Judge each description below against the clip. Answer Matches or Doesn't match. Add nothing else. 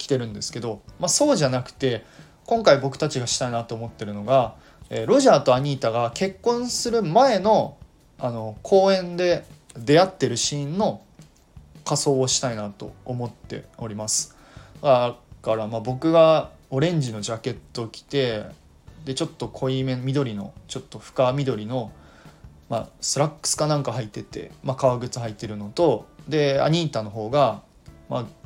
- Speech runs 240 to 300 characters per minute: Doesn't match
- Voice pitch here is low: Matches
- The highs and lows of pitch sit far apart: Doesn't match